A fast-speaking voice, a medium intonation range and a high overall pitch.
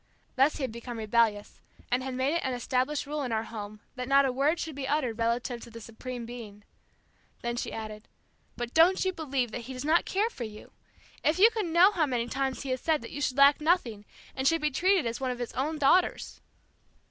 Yes: fast, 230 wpm; average, 4.4 semitones; very high, 260 Hz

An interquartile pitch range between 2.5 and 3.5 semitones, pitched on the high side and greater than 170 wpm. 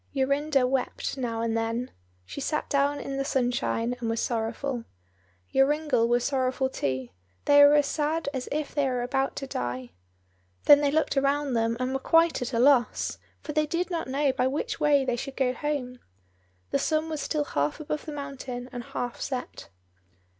Yes: average, 3.0 semitones; very high, 270 Hz; average, 185 wpm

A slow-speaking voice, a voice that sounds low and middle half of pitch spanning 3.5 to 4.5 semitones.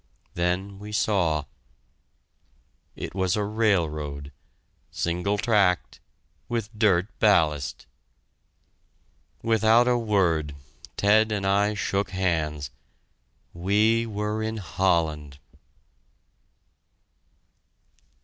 Yes: slow, 80 wpm; low, 100 Hz; average, 4.0 semitones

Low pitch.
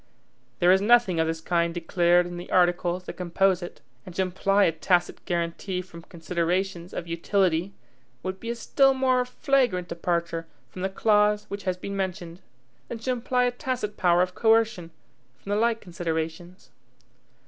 No: medium, 185 Hz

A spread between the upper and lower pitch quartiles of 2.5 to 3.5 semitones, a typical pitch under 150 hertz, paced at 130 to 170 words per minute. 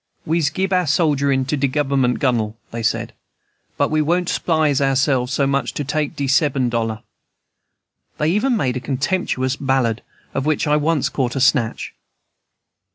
Yes: average, 3.0 semitones; medium, 140 Hz; average, 160 wpm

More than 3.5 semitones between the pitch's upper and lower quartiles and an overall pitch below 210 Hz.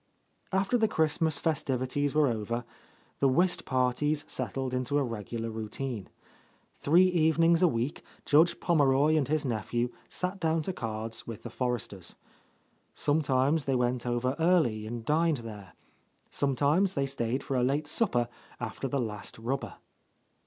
Yes: average, 4.6 semitones; low, 135 Hz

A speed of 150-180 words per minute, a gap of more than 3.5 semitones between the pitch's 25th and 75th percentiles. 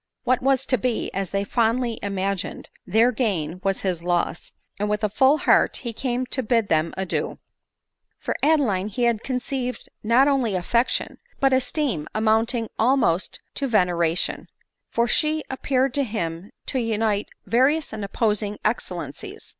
Yes: average, 155 wpm; average, 4.6 semitones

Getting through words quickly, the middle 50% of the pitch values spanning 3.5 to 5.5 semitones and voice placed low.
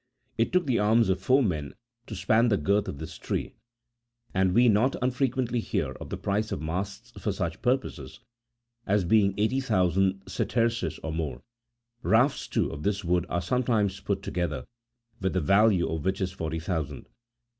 No: average, 170 wpm; average, 4.8 semitones; low, 100 Hz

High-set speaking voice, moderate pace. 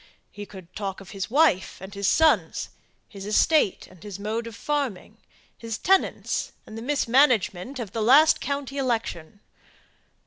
Yes: high, 225 Hz; average, 150 wpm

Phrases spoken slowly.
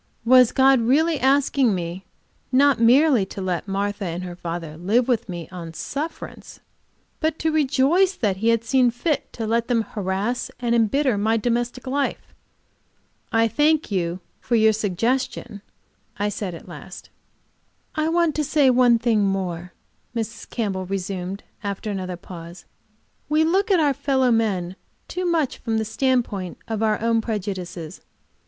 No: average, 155 wpm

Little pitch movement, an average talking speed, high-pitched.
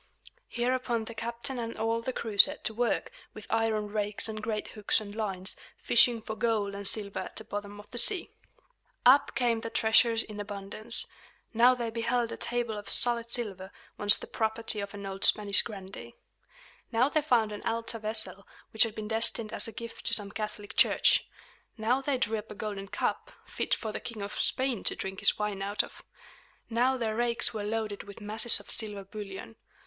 Yes: narrow, 2.2 semitones; average, 195 wpm; high, 220 Hz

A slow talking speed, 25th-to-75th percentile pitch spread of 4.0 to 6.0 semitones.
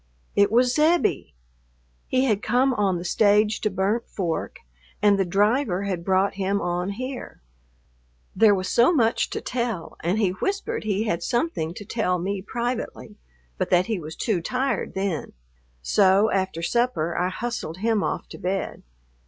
No: average, 160 wpm; average, 4.3 semitones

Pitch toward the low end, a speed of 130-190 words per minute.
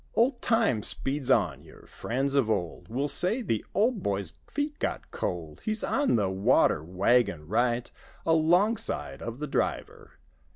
Yes: low, 125 Hz; average, 155 wpm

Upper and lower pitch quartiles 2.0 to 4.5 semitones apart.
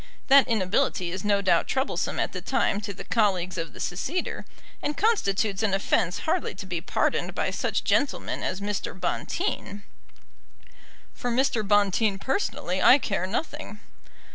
No: average, 5.1 semitones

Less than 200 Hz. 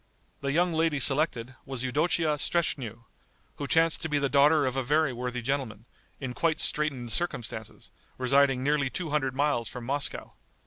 Yes: medium, 140 Hz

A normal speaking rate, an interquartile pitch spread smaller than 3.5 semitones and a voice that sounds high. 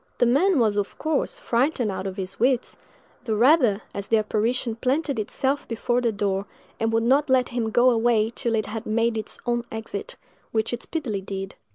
Yes: average, 190 wpm; average, 2.9 semitones; high, 230 Hz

